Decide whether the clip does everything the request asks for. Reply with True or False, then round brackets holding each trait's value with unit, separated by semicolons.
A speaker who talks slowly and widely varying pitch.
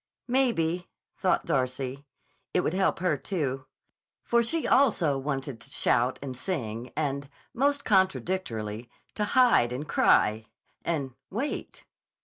True (120 wpm; 7.3 semitones)